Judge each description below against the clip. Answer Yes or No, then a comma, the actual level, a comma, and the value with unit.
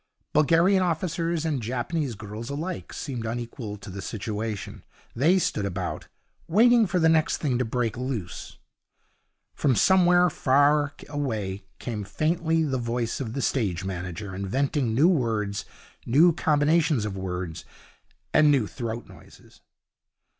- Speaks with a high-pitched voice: No, low, 130 Hz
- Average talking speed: No, slow, 130 wpm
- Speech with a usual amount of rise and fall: No, wide, 6.9 semitones